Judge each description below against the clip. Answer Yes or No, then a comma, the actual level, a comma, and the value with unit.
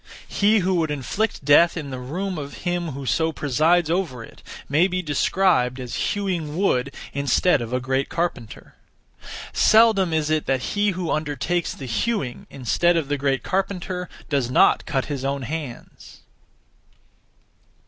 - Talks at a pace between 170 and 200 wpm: No, average, 155 wpm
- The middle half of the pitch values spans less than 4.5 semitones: No, average, 5.0 semitones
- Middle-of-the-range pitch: Yes, medium, 155 Hz